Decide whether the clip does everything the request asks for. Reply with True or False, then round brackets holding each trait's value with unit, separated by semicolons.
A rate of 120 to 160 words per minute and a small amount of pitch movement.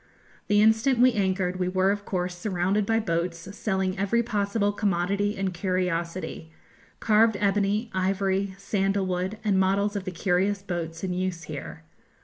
True (150 wpm; 2.1 semitones)